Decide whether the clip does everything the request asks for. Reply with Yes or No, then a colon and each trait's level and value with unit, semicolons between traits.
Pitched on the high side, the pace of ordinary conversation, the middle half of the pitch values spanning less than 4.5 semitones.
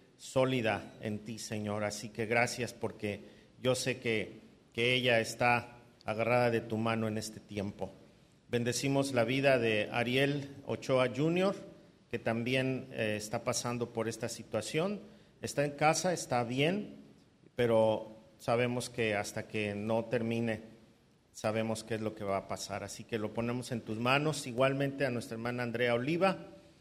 No: low, 115 Hz; average, 155 wpm; average, 2.7 semitones